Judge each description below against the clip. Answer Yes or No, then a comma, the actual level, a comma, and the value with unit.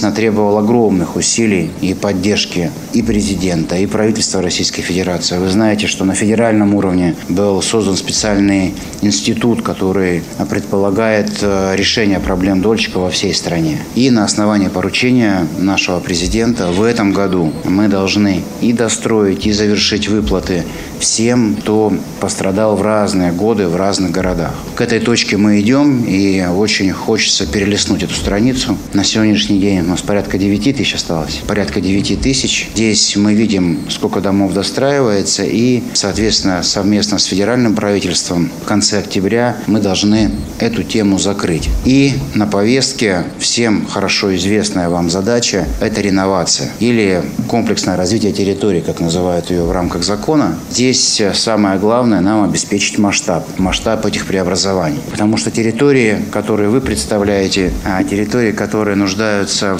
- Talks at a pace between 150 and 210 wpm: No, average, 135 wpm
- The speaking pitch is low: Yes, low, 100 Hz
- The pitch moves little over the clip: Yes, narrow, 2.3 semitones